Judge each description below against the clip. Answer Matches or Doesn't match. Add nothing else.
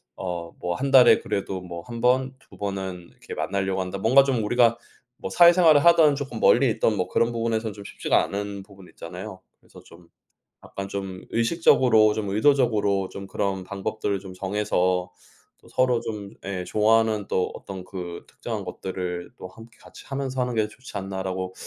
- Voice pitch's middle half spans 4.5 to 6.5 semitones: Doesn't match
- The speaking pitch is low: Matches